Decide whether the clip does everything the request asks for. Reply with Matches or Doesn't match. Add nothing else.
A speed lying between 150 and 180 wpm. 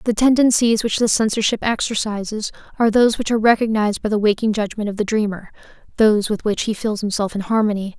Doesn't match